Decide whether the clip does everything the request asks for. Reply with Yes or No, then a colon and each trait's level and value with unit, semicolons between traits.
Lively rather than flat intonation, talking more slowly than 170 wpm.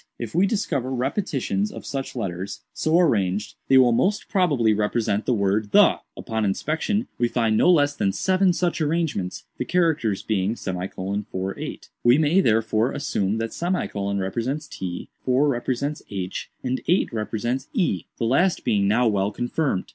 Yes: wide, 6.7 semitones; average, 150 wpm